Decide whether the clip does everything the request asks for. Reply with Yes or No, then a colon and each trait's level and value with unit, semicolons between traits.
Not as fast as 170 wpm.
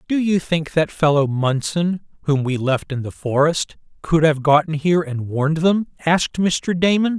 No: average, 185 wpm